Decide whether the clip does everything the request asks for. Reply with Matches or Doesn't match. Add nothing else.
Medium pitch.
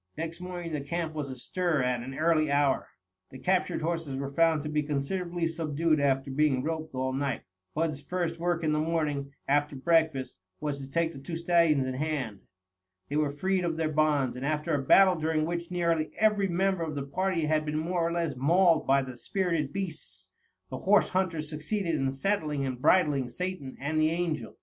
Matches